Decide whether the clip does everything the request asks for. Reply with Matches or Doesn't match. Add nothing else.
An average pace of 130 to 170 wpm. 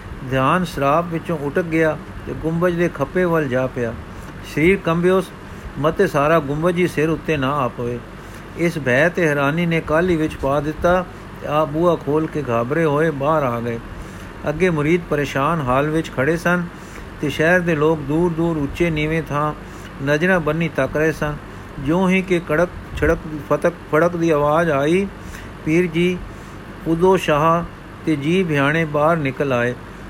Matches